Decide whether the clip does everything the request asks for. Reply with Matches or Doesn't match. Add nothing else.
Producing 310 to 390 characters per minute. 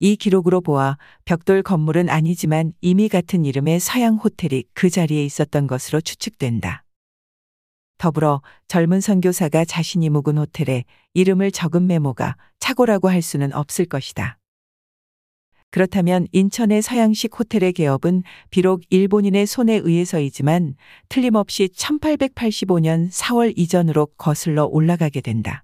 Doesn't match